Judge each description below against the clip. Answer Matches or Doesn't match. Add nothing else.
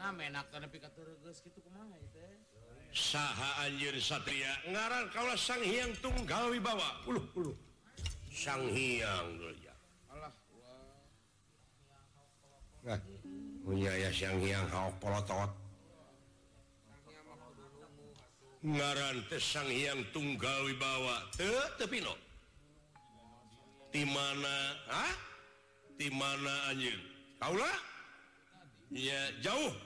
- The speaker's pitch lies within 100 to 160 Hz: Matches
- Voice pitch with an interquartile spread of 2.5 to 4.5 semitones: Doesn't match